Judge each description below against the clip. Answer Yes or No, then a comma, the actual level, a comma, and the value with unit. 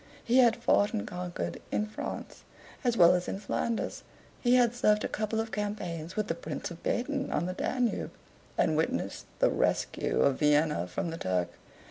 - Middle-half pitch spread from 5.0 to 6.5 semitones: Yes, wide, 5.5 semitones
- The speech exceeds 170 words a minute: Yes, average, 180 wpm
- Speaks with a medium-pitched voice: No, high, 210 Hz